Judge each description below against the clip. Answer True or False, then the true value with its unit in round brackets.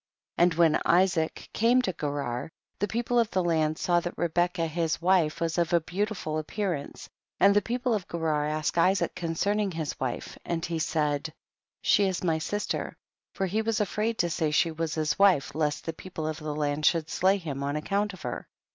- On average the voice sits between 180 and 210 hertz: False (170 Hz)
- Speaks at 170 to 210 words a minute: True (205 wpm)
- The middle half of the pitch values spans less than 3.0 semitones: False (3.7 semitones)